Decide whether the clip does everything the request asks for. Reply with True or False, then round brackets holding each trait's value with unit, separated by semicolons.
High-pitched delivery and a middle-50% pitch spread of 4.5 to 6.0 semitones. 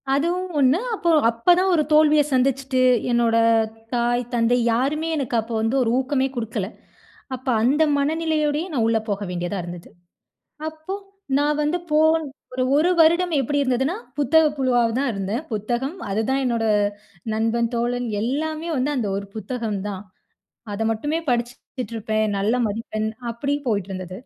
True (250 Hz; 5.0 semitones)